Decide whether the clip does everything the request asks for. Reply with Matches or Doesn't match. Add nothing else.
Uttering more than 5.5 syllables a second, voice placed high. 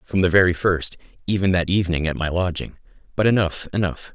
Doesn't match